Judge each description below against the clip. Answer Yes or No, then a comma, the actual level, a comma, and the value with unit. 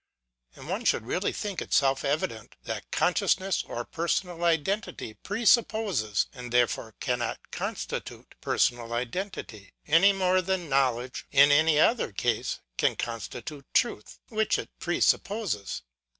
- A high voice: No, medium, 145 Hz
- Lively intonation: Yes, wide, 7.9 semitones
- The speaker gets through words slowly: Yes, slow, 125 wpm